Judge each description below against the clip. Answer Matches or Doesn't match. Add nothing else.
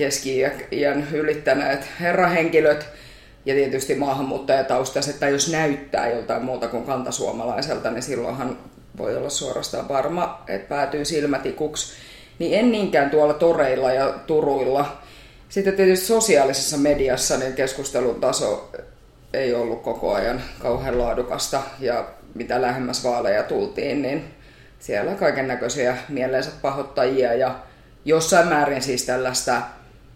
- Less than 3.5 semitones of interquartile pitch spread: Matches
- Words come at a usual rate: Matches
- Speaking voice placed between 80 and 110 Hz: Doesn't match